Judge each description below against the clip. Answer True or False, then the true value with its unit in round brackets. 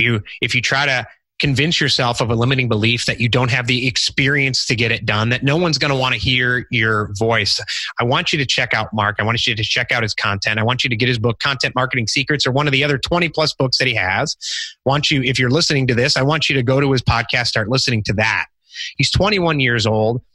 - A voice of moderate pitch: False (125 Hz)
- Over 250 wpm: True (270 wpm)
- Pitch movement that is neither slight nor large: True (3.0 semitones)